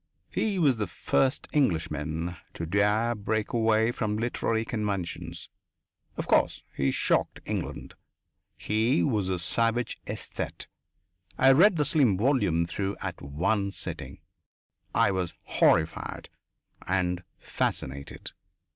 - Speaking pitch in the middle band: No, low, 105 Hz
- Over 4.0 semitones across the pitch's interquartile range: Yes, average, 5.0 semitones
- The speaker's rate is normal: No, slow, 115 wpm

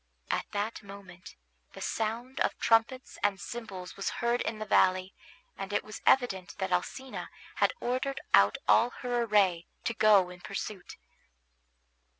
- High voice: Yes, high, 210 Hz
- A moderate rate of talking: Yes, average, 150 wpm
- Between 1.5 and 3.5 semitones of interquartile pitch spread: No, average, 4.0 semitones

